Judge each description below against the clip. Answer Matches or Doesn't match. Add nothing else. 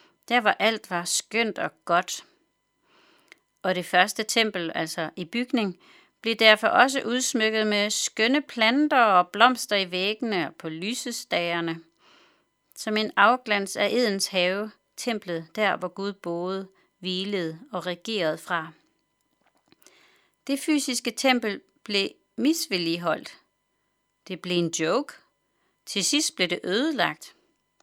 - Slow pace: Matches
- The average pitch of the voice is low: Doesn't match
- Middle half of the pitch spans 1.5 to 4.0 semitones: Doesn't match